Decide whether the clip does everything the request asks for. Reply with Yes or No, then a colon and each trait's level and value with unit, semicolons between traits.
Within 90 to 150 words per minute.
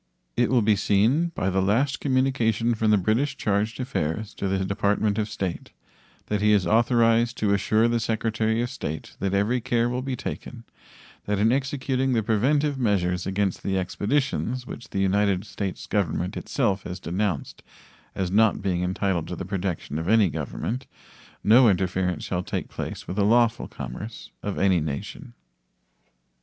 No: average, 165 wpm